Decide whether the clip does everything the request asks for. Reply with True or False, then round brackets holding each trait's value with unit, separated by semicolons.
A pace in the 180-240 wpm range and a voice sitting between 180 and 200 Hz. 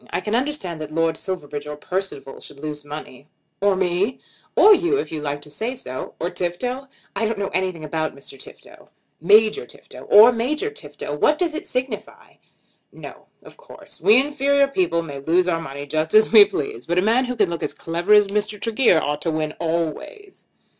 True (195 wpm; 185 Hz)